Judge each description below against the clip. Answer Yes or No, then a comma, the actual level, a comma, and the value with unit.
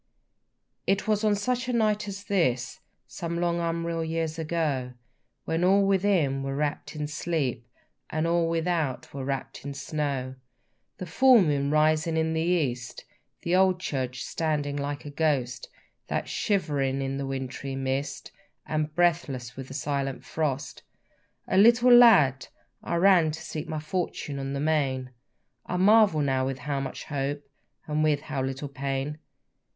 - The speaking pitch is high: No, medium, 150 Hz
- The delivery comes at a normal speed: Yes, average, 155 wpm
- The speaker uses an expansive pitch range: No, average, 4.0 semitones